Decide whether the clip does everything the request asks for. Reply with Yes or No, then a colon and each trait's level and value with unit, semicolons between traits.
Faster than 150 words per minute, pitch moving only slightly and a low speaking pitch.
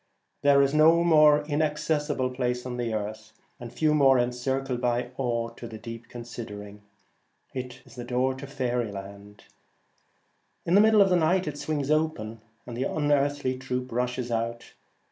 No: average, 165 wpm; average, 3.8 semitones; low, 125 Hz